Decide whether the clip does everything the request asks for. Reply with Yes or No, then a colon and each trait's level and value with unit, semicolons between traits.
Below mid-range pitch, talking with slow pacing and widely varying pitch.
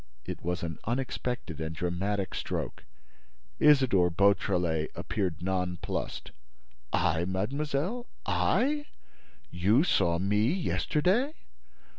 Yes: low, 100 Hz; slow, 90 wpm; wide, 7.8 semitones